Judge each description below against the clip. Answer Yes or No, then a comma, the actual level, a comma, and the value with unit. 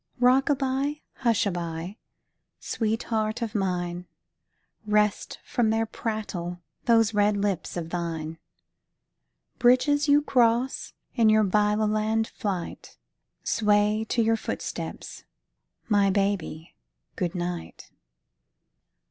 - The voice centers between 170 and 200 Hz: No, high, 215 Hz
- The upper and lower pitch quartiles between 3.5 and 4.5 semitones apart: Yes, average, 3.9 semitones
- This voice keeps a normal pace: No, slow, 105 wpm